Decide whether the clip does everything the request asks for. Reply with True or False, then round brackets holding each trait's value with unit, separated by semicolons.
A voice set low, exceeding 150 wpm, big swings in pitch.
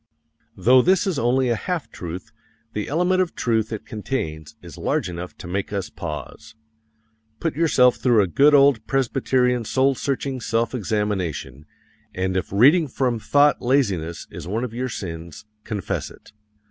True (115 Hz; 160 wpm; 6.2 semitones)